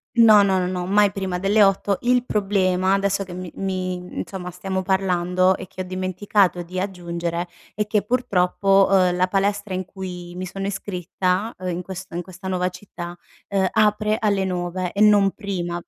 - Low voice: No, high, 190 Hz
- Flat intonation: Yes, narrow, 1.8 semitones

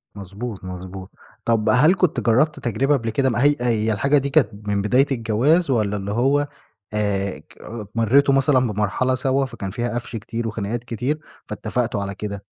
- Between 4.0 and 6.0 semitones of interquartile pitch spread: Yes, average, 4.5 semitones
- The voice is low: Yes, low, 115 Hz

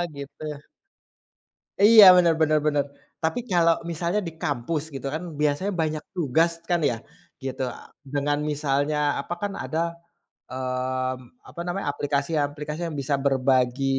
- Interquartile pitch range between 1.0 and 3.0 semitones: No, average, 3.4 semitones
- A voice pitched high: No, medium, 145 Hz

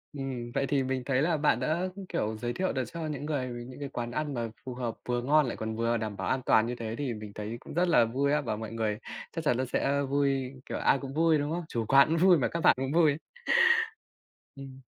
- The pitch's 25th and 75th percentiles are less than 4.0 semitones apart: Yes, average, 3.6 semitones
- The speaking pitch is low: Yes, low, 130 Hz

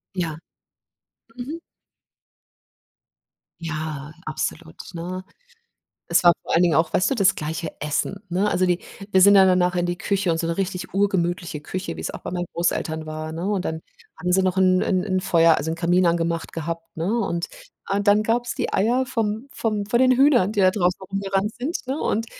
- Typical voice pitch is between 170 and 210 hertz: Yes, medium, 185 Hz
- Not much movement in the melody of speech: No, average, 3.3 semitones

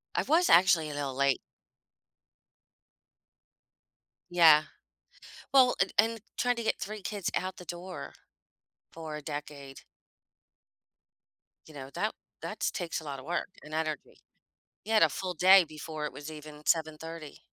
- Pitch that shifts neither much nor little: Yes, average, 4.1 semitones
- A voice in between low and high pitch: Yes, medium, 160 Hz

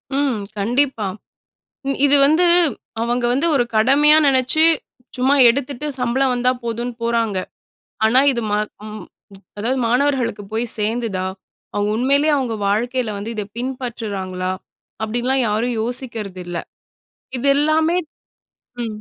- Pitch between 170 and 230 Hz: No, high, 245 Hz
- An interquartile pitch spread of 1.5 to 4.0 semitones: Yes, average, 3.5 semitones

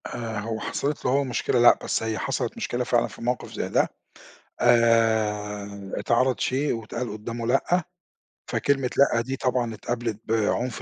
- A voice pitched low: Yes, low, 120 Hz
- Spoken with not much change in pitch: Yes, narrow, 2.3 semitones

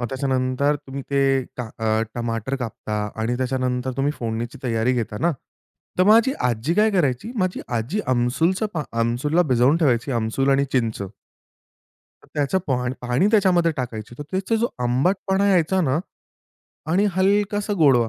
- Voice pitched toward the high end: No, low, 135 Hz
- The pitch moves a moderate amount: No, wide, 6.6 semitones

